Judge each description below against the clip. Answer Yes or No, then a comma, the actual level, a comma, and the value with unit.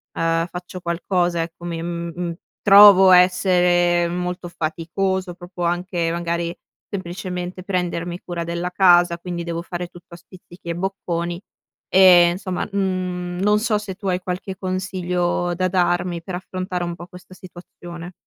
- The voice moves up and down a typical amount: No, narrow, 1.3 semitones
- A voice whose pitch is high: No, medium, 175 Hz